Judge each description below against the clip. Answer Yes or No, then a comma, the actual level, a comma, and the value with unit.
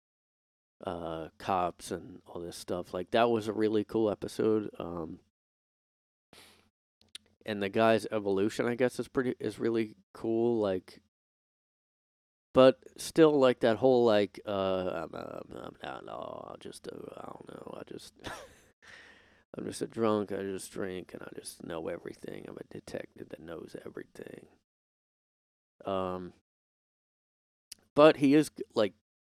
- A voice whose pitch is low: Yes, low, 110 Hz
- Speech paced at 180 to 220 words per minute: No, average, 140 wpm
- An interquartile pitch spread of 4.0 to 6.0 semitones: Yes, average, 4.3 semitones